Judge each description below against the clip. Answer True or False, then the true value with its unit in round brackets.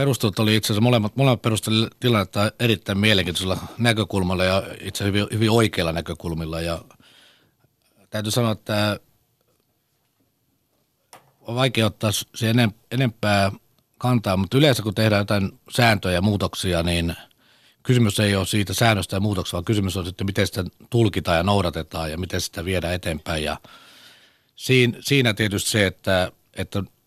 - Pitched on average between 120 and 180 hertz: False (105 Hz)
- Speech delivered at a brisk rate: False (140 wpm)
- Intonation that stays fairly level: False (3.5 semitones)